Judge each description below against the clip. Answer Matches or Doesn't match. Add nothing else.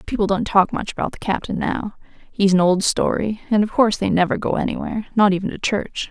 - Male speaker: Doesn't match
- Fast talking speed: Matches